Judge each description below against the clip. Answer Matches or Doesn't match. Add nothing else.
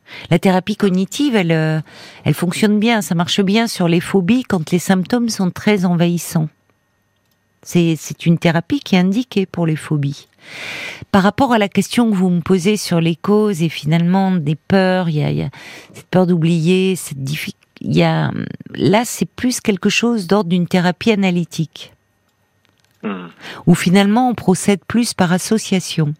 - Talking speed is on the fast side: Doesn't match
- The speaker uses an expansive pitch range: Doesn't match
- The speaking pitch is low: Doesn't match